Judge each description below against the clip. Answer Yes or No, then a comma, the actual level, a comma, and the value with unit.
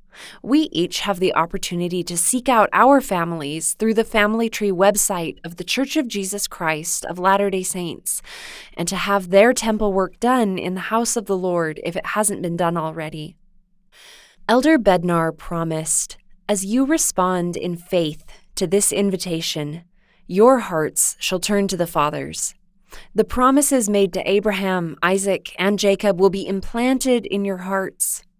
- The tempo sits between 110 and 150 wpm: No, average, 160 wpm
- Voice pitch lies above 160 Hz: Yes, high, 190 Hz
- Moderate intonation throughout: Yes, average, 3.3 semitones